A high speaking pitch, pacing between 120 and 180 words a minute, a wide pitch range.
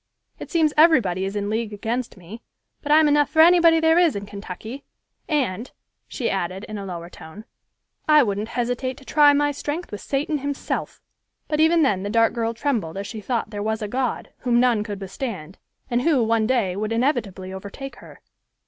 No: high, 230 Hz; average, 195 wpm; wide, 6.0 semitones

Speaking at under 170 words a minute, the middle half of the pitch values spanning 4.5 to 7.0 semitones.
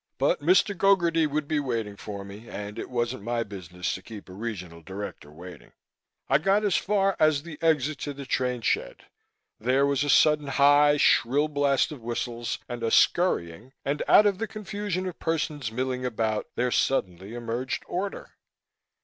No: average, 175 wpm; wide, 5.5 semitones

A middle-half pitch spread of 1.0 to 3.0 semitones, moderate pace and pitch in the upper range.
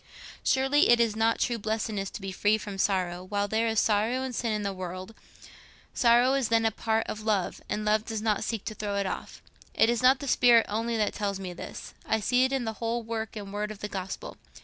No: narrow, 2.4 semitones; fast, 235 wpm; high, 220 Hz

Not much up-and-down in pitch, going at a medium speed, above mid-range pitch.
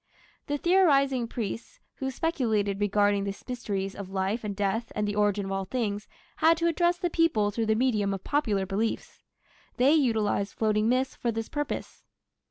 No: average, 4.7 semitones; average, 175 wpm; high, 220 Hz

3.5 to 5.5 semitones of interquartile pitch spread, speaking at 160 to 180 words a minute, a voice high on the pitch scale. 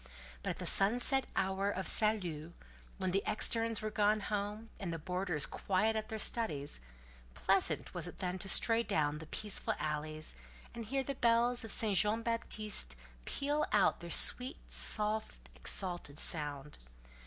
Yes: average, 4.7 semitones; average, 165 wpm; high, 200 Hz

